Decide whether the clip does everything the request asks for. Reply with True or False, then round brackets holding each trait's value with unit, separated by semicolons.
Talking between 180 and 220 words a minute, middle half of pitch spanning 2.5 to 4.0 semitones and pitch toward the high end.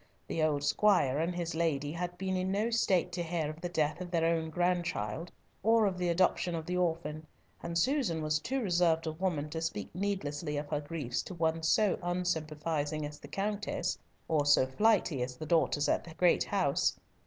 False (200 wpm; 2.9 semitones; 165 Hz)